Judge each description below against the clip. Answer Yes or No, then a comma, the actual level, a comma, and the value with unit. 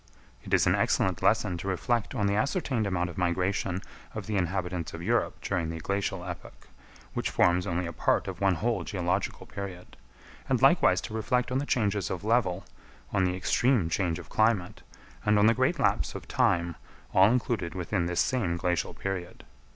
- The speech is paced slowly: No, average, 185 wpm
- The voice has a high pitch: No, very low, 95 Hz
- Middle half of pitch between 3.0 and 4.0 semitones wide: Yes, average, 3.4 semitones